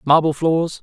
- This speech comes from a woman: No, male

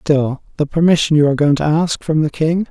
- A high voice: No, medium, 155 Hz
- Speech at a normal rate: No, fast, 245 wpm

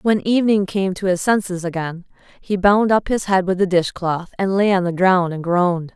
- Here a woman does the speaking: Yes, female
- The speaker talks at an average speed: No, fast, 220 wpm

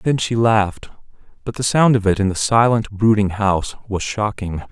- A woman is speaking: No, male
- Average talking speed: Yes, average, 190 wpm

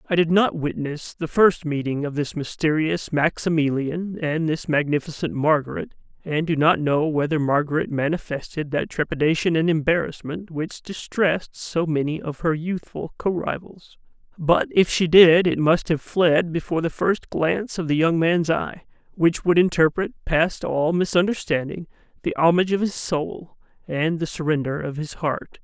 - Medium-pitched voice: Yes, medium, 160 Hz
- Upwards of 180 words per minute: No, average, 160 wpm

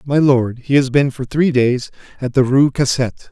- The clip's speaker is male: Yes, male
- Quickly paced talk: Yes, fast, 215 wpm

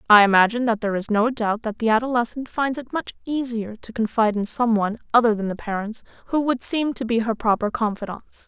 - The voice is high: Yes, high, 230 Hz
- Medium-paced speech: No, fast, 220 wpm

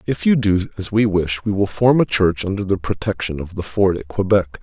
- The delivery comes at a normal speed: No, fast, 245 wpm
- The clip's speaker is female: No, male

